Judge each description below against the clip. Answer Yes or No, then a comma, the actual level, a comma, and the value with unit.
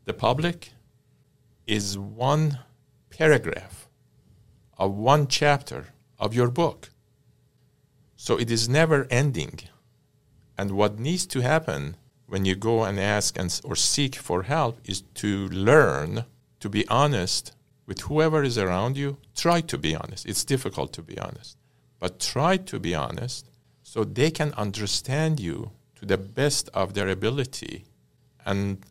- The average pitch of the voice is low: Yes, low, 125 Hz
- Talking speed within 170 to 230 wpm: No, average, 140 wpm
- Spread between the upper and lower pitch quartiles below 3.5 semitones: No, average, 5.2 semitones